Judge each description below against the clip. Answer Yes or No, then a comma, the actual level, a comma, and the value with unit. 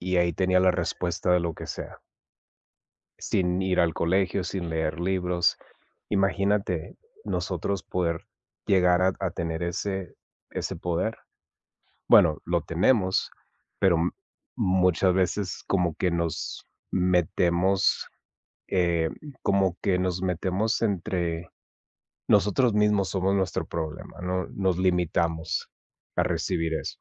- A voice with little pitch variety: Yes, narrow, 1.9 semitones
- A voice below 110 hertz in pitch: Yes, very low, 90 Hz